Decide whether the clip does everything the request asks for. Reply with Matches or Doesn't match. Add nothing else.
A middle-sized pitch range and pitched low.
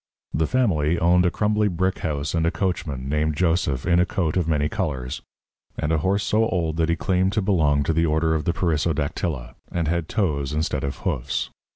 Matches